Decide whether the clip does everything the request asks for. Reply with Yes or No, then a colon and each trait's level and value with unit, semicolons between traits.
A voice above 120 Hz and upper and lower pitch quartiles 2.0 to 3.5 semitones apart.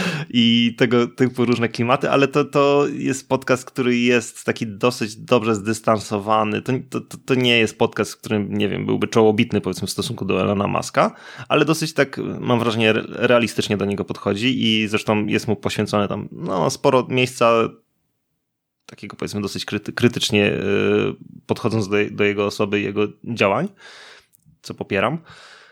No: low, 115 Hz; average, 3.1 semitones